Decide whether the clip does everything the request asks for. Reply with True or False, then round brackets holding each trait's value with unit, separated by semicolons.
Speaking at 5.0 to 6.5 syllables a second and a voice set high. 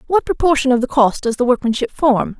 True (5.8 syllables/s; 265 Hz)